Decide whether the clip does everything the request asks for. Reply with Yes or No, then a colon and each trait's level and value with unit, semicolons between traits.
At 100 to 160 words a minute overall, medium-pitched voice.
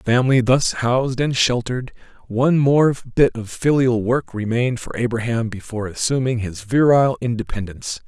No: average, 150 wpm; low, 120 Hz